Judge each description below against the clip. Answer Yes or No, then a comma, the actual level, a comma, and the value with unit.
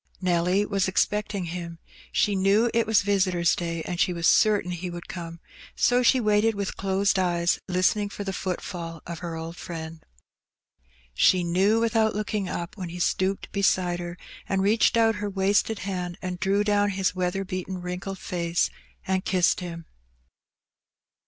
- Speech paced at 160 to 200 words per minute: Yes, average, 165 wpm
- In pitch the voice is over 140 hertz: Yes, medium, 185 Hz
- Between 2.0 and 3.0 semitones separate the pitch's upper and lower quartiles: Yes, narrow, 2.6 semitones